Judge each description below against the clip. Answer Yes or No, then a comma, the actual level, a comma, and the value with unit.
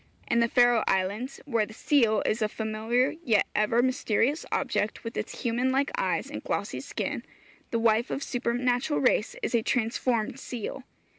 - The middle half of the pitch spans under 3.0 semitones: Yes, narrow, 2.6 semitones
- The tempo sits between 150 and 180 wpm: Yes, average, 165 wpm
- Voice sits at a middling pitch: No, high, 235 Hz